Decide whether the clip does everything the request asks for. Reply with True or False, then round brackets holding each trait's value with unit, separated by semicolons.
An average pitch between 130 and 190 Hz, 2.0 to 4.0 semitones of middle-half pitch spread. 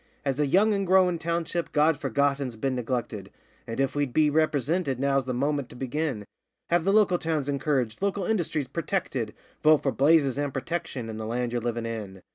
False (140 Hz; 4.7 semitones)